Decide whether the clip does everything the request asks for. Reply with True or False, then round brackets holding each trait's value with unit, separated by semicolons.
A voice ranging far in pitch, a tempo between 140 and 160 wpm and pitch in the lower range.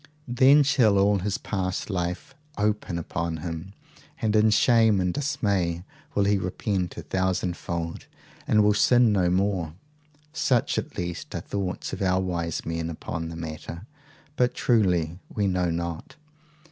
False (3.5 semitones; 150 wpm; 95 Hz)